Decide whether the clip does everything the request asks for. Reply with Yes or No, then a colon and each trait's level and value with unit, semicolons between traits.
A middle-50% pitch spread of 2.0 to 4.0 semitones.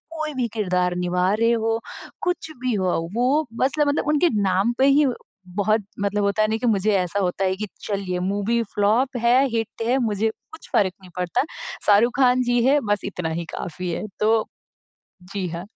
No: average, 4.7 semitones